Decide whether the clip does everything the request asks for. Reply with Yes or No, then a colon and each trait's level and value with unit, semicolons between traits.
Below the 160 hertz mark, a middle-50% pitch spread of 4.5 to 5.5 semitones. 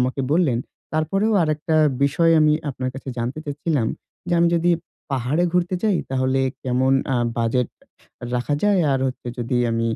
Yes: medium, 140 Hz; average, 4.8 semitones